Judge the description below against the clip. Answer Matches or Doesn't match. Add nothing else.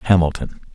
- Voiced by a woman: Doesn't match